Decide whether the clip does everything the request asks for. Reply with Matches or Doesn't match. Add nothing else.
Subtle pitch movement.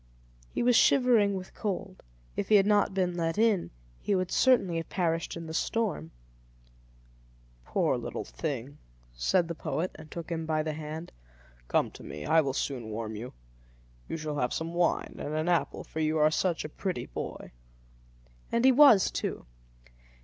Doesn't match